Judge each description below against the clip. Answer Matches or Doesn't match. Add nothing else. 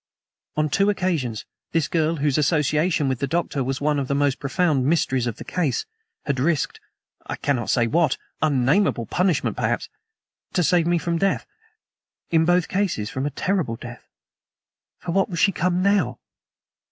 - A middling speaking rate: Matches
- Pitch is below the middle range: Doesn't match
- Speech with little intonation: Doesn't match